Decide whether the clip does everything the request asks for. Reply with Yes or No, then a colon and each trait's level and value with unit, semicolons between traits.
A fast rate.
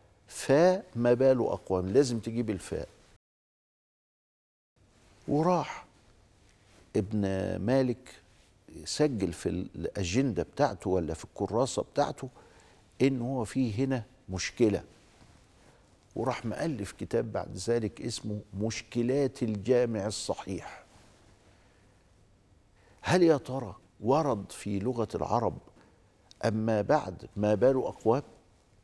No: average, 90 wpm